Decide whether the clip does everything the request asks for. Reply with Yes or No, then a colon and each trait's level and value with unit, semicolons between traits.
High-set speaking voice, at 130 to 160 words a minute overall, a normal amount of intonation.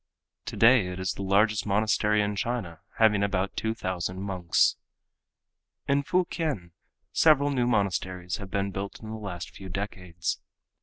No: low, 100 Hz; average, 145 wpm; average, 3.1 semitones